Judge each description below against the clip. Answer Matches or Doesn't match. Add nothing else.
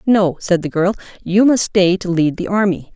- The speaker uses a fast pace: Matches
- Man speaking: Doesn't match